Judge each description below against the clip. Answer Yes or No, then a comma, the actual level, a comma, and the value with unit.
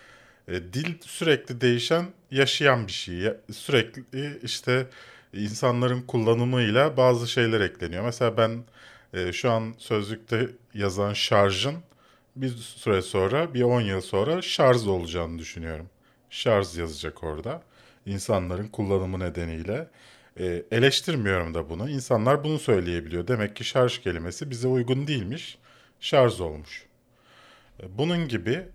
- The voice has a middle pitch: No, low, 115 Hz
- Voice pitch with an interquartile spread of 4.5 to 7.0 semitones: Yes, wide, 5.4 semitones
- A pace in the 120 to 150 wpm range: No, average, 110 wpm